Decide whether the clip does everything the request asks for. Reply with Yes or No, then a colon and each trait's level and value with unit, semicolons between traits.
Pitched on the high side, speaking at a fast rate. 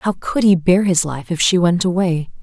No: medium, 175 Hz; fast, 250 wpm